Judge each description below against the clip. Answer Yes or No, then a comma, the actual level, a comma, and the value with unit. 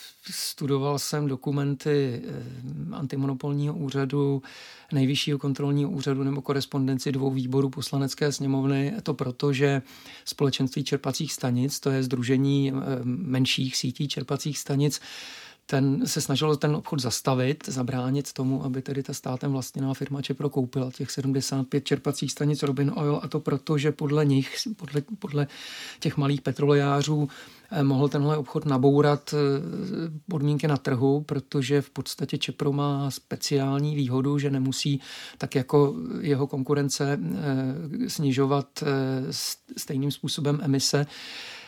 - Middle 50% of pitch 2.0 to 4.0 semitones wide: No, narrow, 1.3 semitones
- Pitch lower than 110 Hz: No, medium, 140 Hz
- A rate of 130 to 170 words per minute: No, average, 120 wpm